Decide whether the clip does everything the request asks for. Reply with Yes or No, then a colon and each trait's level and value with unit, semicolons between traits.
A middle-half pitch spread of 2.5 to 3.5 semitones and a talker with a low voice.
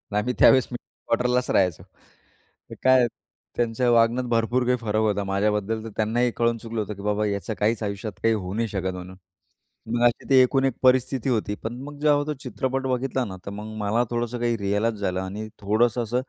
Yes: average, 3.0 semitones; low, 115 Hz